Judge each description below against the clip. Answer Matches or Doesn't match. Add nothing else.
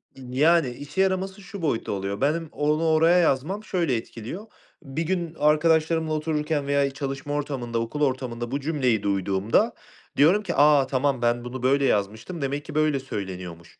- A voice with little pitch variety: Doesn't match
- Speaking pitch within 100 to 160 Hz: Matches